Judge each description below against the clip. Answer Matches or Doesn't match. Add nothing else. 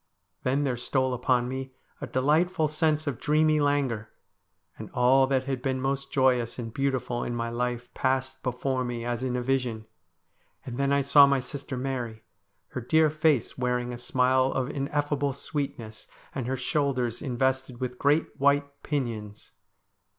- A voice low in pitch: Matches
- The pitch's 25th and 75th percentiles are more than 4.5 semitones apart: Doesn't match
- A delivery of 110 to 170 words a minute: Matches